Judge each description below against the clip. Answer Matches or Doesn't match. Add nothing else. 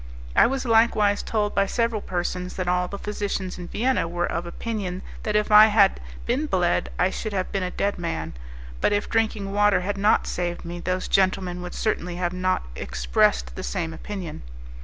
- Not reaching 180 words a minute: Doesn't match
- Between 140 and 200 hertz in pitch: Matches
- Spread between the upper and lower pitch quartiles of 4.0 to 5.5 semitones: Doesn't match